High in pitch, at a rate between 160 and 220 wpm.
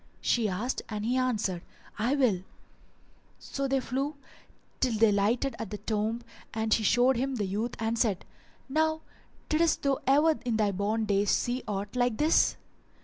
Yes: high, 230 Hz; average, 165 wpm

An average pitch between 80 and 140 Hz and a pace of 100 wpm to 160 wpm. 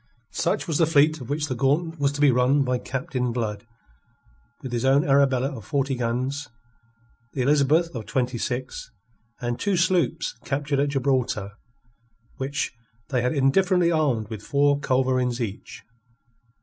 Yes: low, 135 Hz; average, 150 wpm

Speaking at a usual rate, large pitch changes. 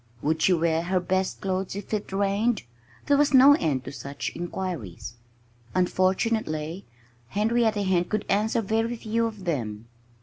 No: average, 145 wpm; average, 4.7 semitones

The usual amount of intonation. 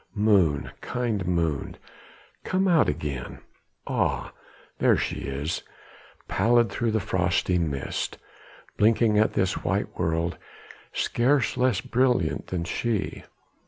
No: wide, 6.0 semitones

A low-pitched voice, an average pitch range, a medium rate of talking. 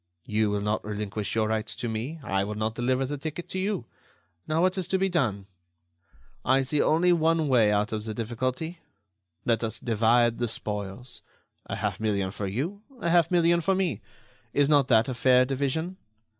No: low, 125 Hz; wide, 6.8 semitones; average, 190 wpm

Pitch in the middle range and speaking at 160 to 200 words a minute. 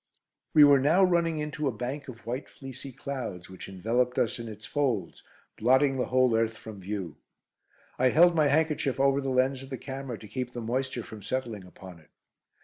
No: low, 130 Hz; average, 195 wpm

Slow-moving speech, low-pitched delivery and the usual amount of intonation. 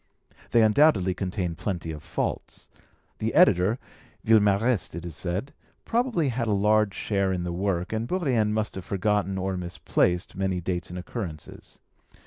No: average, 150 wpm; very low, 95 Hz; average, 3.7 semitones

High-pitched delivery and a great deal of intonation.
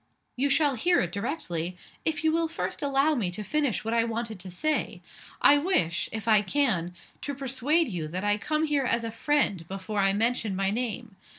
Yes: high, 230 Hz; wide, 6.8 semitones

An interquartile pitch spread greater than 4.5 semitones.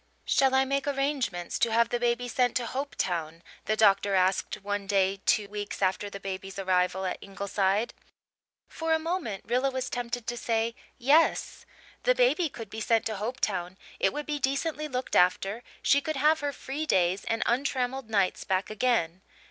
Yes: wide, 5.5 semitones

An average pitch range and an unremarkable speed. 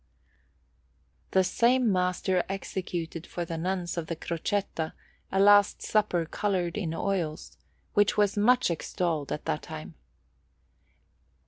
No: average, 3.5 semitones; slow, 120 wpm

